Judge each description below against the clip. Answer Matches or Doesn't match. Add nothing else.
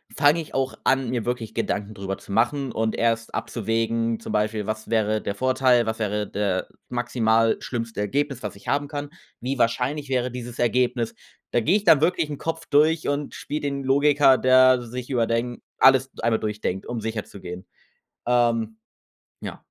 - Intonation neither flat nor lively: Matches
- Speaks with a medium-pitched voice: Doesn't match